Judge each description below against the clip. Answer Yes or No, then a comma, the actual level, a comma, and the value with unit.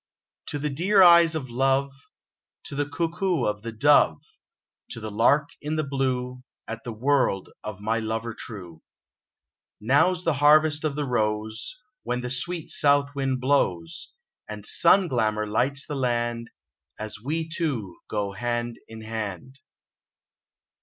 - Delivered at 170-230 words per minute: No, average, 145 wpm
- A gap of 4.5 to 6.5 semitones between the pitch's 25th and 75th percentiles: Yes, average, 4.9 semitones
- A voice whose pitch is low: Yes, low, 125 Hz